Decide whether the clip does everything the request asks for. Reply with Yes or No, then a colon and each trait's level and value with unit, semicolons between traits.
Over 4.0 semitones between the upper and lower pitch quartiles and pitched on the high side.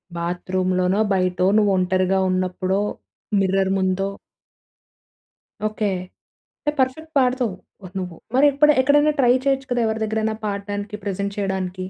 Yes: average, 4.5 semitones; high, 200 Hz